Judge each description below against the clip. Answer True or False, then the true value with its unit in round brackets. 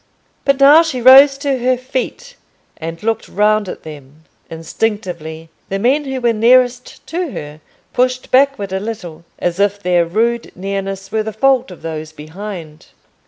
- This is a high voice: True (215 Hz)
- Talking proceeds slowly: False (160 wpm)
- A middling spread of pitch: False (6.8 semitones)